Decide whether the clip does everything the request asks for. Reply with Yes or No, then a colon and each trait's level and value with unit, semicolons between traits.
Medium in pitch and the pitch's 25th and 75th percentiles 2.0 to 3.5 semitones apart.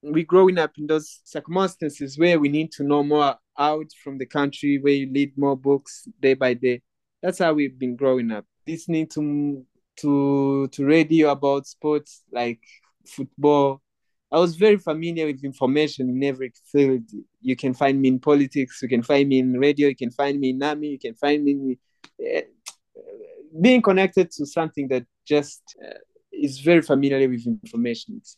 Yes: medium, 145 Hz; average, 2.9 semitones